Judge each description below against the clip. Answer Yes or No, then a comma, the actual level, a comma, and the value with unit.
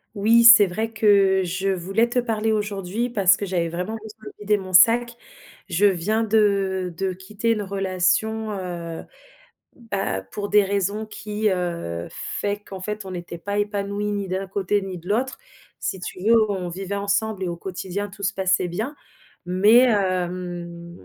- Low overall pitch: No, high, 200 Hz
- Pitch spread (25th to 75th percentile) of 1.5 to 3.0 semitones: Yes, narrow, 2.6 semitones